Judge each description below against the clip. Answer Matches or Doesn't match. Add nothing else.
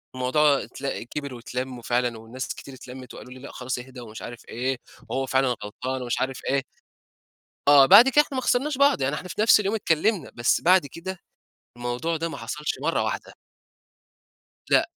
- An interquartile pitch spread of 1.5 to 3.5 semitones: Doesn't match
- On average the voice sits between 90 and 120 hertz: Doesn't match